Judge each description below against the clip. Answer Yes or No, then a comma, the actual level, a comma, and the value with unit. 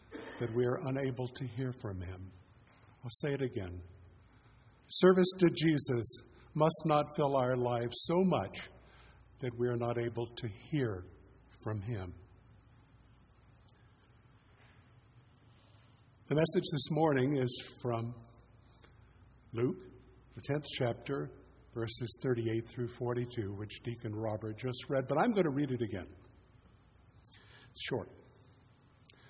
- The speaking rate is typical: No, slow, 120 wpm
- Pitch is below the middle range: Yes, low, 120 Hz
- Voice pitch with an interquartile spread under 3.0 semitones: Yes, narrow, 2.4 semitones